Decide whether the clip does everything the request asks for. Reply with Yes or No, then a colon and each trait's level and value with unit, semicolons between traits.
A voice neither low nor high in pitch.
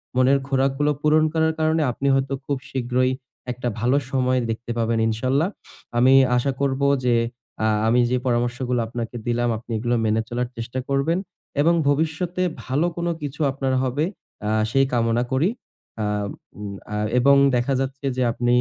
No: low, 130 Hz